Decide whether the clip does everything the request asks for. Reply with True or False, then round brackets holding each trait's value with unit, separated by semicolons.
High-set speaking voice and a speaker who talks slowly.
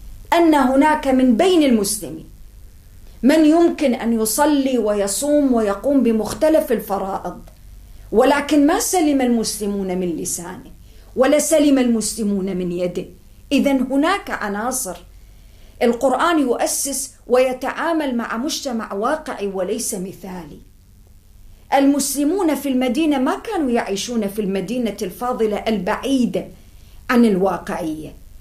True (235 Hz; 100 wpm)